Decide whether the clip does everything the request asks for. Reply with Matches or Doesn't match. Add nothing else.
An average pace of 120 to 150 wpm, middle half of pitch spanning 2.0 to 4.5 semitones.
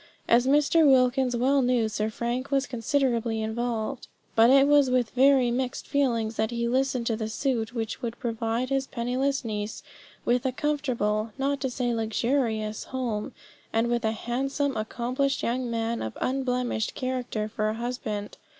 Doesn't match